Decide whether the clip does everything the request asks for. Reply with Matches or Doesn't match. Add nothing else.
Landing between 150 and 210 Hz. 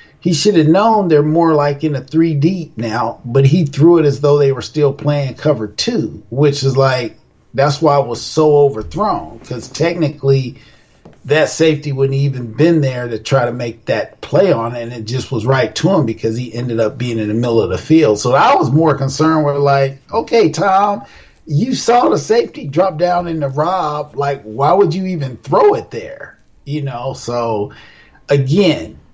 Doesn't match